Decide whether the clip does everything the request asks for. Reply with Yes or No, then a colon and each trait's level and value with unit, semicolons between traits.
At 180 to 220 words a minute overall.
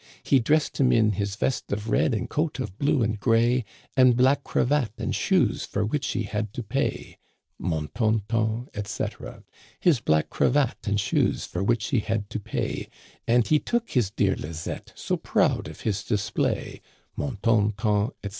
Yes: average, 185 wpm